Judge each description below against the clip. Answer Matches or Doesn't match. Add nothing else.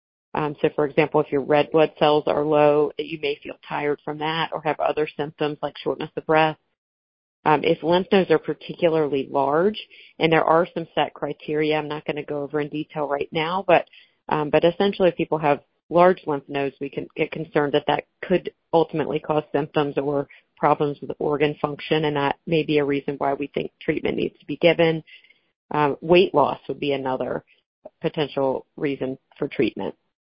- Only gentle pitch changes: Matches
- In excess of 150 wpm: Matches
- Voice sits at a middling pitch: Matches